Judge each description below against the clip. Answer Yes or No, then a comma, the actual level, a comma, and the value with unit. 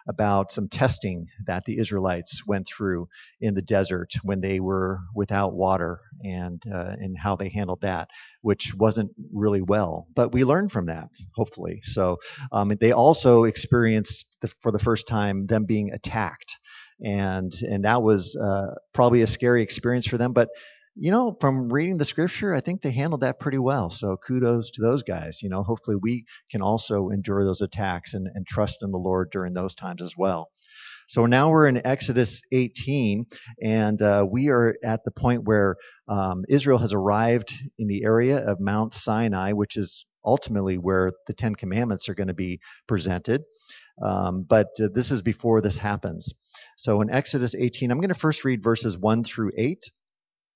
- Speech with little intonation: No, average, 3.8 semitones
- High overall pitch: No, low, 105 Hz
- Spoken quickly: No, average, 180 wpm